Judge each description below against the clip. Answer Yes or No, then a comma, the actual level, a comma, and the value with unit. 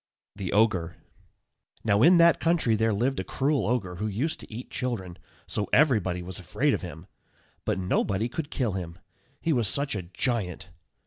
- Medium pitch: No, low, 110 Hz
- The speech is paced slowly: No, average, 175 wpm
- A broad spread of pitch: Yes, wide, 6.2 semitones